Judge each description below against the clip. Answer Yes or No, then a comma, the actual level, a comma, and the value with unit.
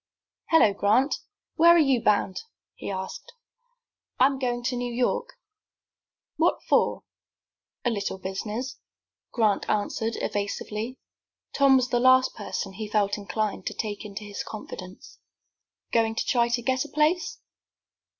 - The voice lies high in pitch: Yes, high, 235 Hz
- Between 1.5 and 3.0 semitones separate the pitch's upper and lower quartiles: No, average, 4.1 semitones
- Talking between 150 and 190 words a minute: No, average, 140 wpm